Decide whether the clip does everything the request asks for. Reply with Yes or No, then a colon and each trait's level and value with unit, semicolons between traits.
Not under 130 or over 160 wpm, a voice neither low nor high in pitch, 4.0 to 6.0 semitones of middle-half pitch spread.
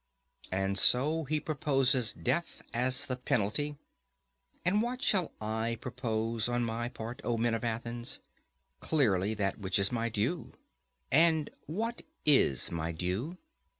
No: slow, 135 wpm; low, 120 Hz; average, 5.2 semitones